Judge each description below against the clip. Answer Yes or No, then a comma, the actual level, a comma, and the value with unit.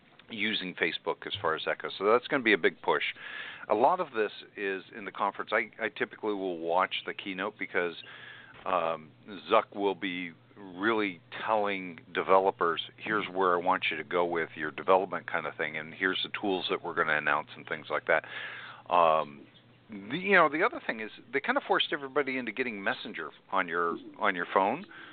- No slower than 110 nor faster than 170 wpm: No, average, 200 wpm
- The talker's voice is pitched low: Yes, very low, 95 Hz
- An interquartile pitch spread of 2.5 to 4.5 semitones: No, average, 4.9 semitones